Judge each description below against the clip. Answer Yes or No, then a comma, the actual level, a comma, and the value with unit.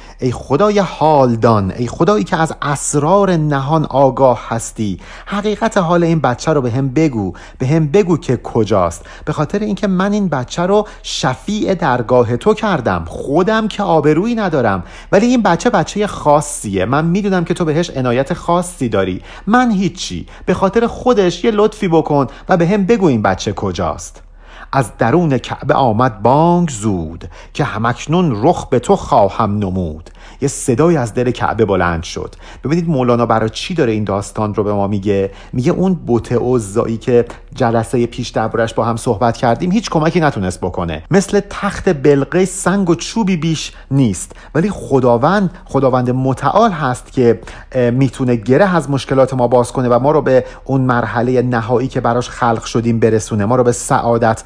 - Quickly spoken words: Yes, fast, 165 wpm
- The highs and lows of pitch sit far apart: Yes, wide, 7.2 semitones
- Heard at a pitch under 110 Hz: No, low, 130 Hz